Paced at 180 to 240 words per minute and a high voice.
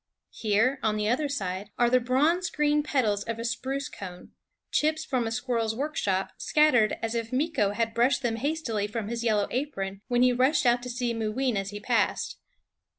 Yes: average, 190 wpm; high, 240 Hz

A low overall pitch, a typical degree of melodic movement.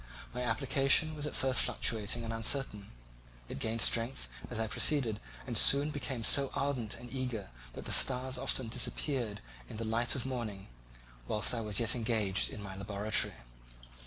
Yes: low, 115 Hz; average, 3.6 semitones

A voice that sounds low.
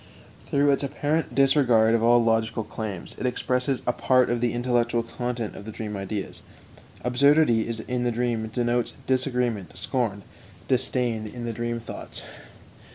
Yes: low, 120 Hz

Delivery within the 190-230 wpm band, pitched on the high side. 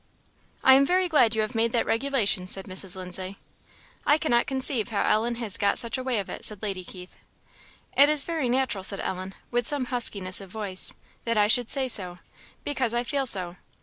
Yes: fast, 205 wpm; high, 230 Hz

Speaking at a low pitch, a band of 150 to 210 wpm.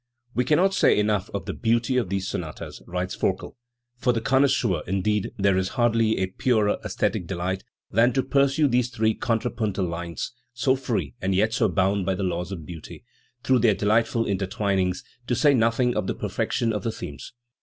Yes: low, 105 Hz; average, 185 wpm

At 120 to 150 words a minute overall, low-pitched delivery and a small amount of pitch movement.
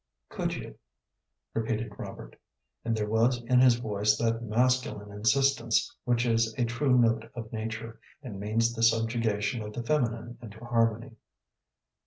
Yes: average, 145 wpm; low, 115 Hz; narrow, 1.4 semitones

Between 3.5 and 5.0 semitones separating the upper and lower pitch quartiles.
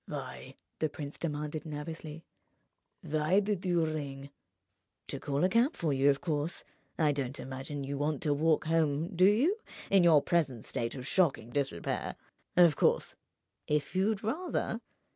Yes: average, 3.8 semitones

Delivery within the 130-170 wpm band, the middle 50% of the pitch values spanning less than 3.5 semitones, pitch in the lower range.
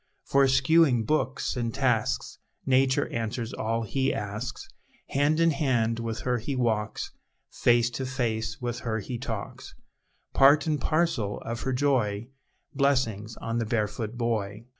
Yes: average, 140 wpm; average, 3.1 semitones; low, 120 Hz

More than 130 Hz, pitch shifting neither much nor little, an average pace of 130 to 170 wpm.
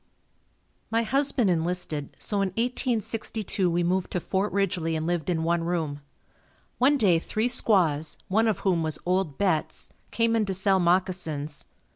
Yes: medium, 185 Hz; average, 4.4 semitones; average, 155 wpm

